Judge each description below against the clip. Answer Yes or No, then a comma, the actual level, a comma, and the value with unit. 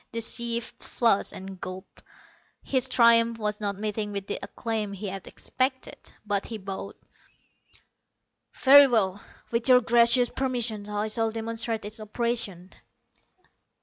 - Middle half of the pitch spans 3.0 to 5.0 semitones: No, narrow, 2.6 semitones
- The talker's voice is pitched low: No, high, 220 Hz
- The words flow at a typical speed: No, slow, 130 wpm